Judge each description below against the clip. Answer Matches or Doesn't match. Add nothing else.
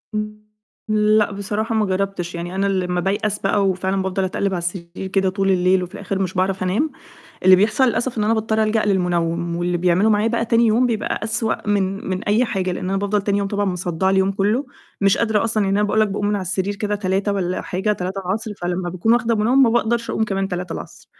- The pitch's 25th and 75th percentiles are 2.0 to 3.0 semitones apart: Matches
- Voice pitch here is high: Matches